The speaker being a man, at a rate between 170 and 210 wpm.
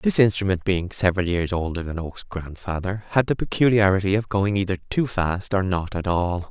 Yes: male; average, 195 wpm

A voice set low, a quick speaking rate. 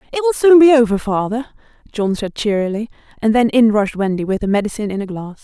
No: high, 225 Hz; fast, 220 wpm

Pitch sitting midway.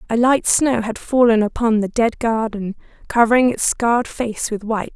No: high, 230 Hz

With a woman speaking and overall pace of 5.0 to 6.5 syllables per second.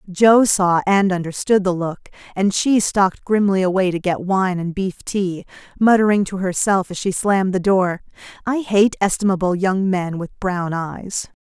No: female; 4.5 syllables/s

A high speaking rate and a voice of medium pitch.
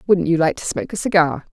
Yes: fast, 270 wpm; medium, 180 Hz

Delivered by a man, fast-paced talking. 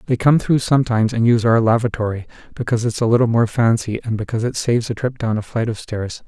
Yes: male; fast, 240 wpm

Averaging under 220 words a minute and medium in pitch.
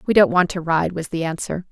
No: fast, 280 wpm; medium, 175 Hz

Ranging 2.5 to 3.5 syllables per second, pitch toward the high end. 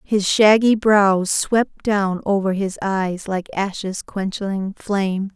Yes: 3.3 syllables/s; high, 195 Hz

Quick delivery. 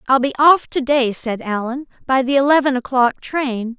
No: average, 190 wpm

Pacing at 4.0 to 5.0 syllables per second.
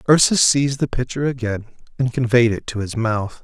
No: 5.5 syllables/s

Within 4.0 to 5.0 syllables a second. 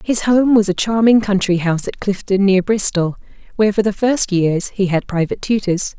No: 5.3 syllables/s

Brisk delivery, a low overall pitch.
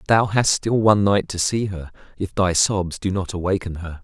Yes: fast, 225 wpm; very low, 95 Hz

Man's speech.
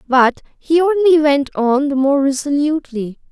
No: female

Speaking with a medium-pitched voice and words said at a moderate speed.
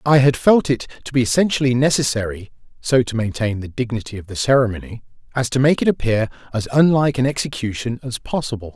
No: low, 120 Hz; average, 185 wpm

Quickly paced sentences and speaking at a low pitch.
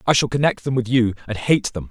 Yes: fast, 285 wpm; low, 120 Hz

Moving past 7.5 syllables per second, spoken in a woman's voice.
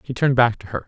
No: 7.8 syllables/s; male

